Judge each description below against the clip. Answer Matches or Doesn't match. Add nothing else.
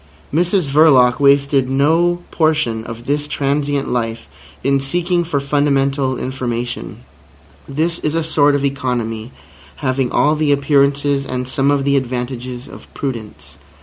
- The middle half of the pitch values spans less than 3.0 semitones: Matches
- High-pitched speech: Doesn't match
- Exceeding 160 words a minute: Doesn't match